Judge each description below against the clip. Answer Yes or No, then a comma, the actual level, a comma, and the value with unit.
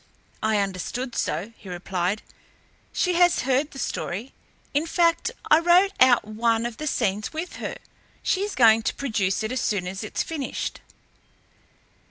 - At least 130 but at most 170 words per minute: Yes, average, 160 wpm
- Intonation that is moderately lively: No, wide, 6.8 semitones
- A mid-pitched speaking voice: No, high, 235 Hz